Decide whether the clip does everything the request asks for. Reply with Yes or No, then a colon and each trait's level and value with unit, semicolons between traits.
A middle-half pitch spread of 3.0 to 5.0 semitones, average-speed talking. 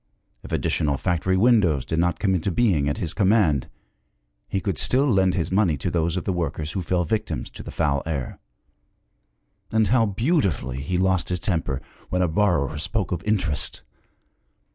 Yes: average, 4.2 semitones; average, 175 wpm